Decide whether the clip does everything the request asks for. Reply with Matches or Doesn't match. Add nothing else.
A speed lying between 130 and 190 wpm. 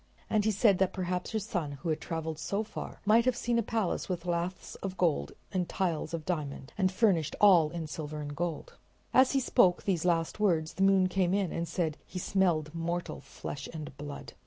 Doesn't match